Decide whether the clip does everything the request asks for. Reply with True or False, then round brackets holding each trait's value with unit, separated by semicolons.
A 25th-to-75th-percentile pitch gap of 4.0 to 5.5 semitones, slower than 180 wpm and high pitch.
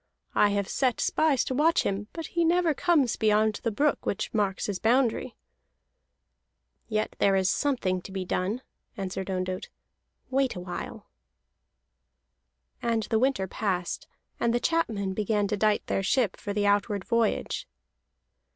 True (4.7 semitones; 145 wpm; 215 Hz)